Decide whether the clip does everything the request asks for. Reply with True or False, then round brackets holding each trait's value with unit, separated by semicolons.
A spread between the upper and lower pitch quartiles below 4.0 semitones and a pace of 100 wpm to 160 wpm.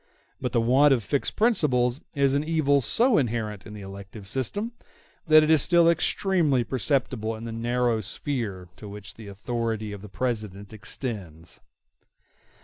False (5.2 semitones; 155 wpm)